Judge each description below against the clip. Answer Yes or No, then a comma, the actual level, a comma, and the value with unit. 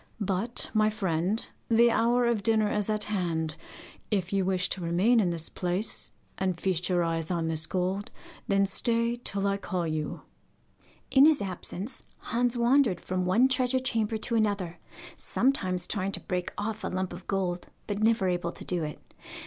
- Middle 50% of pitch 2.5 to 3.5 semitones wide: No, average, 4.1 semitones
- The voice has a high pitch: Yes, high, 195 Hz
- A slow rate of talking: No, average, 180 wpm